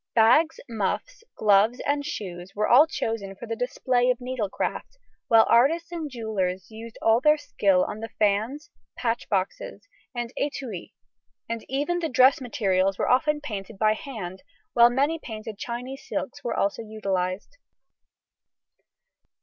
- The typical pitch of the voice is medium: No, high, 230 Hz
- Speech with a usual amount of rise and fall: Yes, average, 4.7 semitones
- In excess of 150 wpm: No, average, 140 wpm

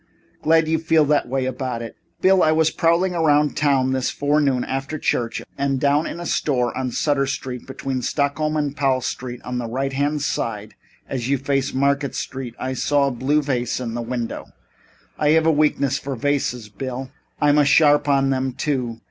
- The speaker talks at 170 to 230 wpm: Yes, average, 190 wpm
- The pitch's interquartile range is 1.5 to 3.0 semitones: Yes, narrow, 2.5 semitones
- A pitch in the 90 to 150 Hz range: Yes, medium, 140 Hz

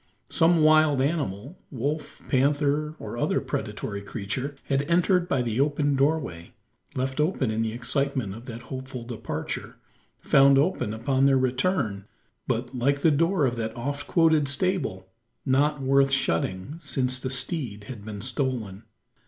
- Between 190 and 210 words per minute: No, average, 145 wpm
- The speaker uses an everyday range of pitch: Yes, average, 3.9 semitones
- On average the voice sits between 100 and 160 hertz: Yes, low, 135 Hz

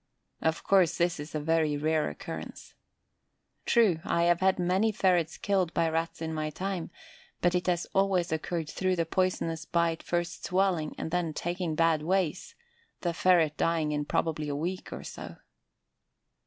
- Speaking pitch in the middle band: Yes, medium, 170 Hz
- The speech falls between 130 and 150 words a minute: No, average, 165 wpm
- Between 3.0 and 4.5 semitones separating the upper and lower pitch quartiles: No, narrow, 2.4 semitones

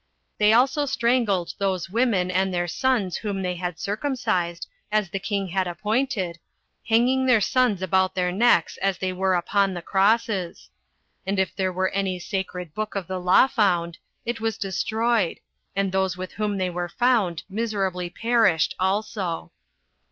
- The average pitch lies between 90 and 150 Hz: No, high, 195 Hz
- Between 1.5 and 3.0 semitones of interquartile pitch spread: No, average, 3.4 semitones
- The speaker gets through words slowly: No, average, 160 wpm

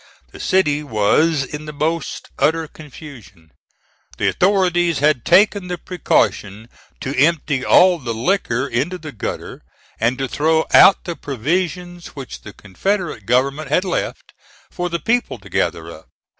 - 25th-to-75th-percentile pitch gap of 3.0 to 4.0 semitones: No, wide, 5.6 semitones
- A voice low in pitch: No, medium, 150 Hz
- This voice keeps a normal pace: Yes, average, 145 wpm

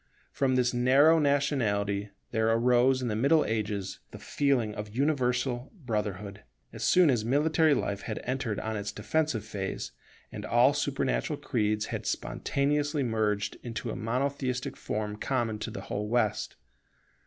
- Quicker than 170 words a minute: No, average, 145 wpm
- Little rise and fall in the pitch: No, average, 4.6 semitones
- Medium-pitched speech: No, low, 120 Hz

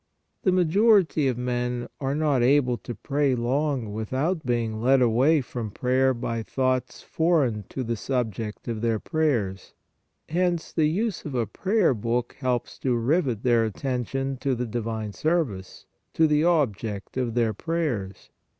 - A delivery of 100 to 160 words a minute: Yes, average, 155 wpm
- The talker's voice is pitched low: Yes, low, 125 Hz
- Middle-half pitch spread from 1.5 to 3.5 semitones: No, average, 4.6 semitones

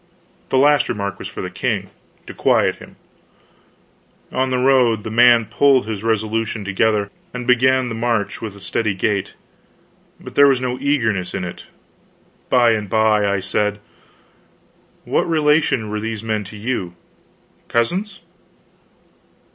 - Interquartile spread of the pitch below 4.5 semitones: Yes, average, 3.5 semitones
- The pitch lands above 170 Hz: No, low, 115 Hz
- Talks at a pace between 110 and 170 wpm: Yes, average, 145 wpm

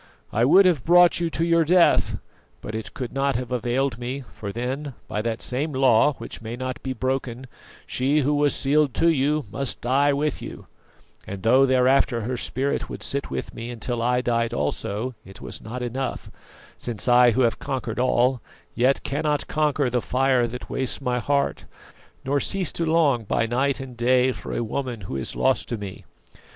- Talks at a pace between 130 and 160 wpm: No, average, 190 wpm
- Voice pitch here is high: No, low, 130 Hz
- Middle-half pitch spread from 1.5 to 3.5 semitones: Yes, average, 2.8 semitones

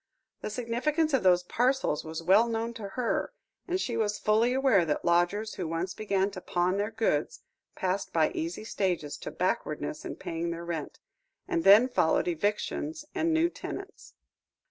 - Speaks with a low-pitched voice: No, high, 205 Hz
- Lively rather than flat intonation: Yes, wide, 5.7 semitones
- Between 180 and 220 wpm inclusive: No, average, 165 wpm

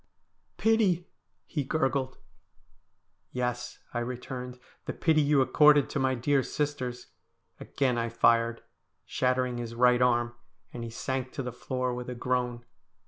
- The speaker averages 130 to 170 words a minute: Yes, average, 155 wpm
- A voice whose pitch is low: Yes, low, 125 Hz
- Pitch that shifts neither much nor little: No, narrow, 2.0 semitones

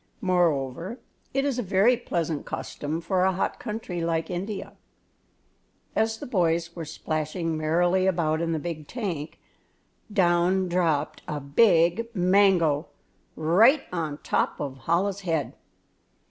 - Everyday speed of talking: No, slow, 130 wpm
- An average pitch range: Yes, average, 3.3 semitones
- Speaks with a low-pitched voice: No, medium, 175 Hz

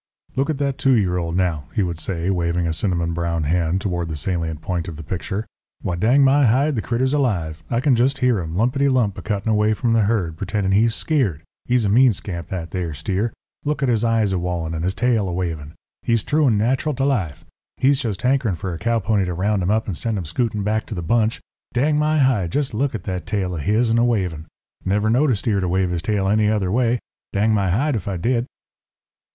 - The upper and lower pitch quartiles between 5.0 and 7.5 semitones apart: Yes, wide, 5.4 semitones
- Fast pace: Yes, fast, 240 wpm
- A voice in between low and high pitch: No, low, 105 Hz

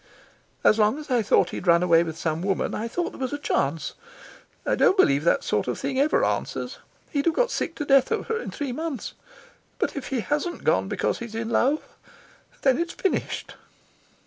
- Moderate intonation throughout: No, wide, 6.6 semitones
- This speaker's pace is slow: No, fast, 205 wpm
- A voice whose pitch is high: Yes, very high, 260 Hz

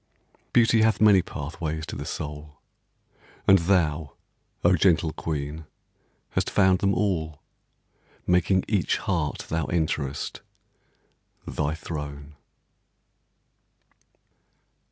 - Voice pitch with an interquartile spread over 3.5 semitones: Yes, average, 3.9 semitones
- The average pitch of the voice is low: Yes, very low, 80 Hz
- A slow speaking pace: Yes, slow, 95 wpm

